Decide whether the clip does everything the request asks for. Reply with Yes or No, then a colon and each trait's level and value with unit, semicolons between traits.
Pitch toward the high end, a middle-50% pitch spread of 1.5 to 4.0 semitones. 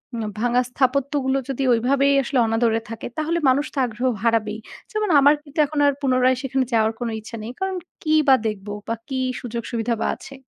Yes: very high, 255 Hz; average, 3.4 semitones